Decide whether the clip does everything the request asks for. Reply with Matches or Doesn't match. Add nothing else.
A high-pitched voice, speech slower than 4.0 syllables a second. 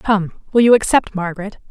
Doesn't match